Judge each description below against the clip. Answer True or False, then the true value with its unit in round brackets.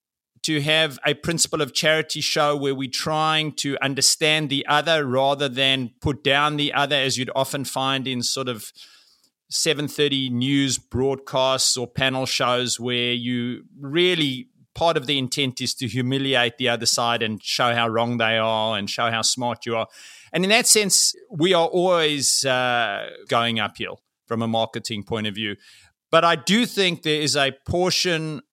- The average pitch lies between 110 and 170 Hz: True (135 Hz)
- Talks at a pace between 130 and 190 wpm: True (170 wpm)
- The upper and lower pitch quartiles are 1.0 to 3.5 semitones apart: False (3.9 semitones)